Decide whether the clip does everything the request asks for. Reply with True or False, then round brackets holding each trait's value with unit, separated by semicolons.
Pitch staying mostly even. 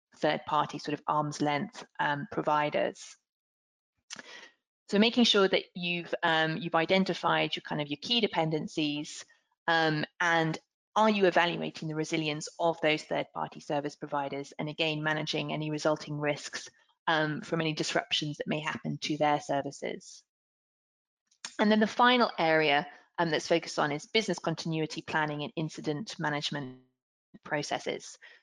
True (2.3 semitones)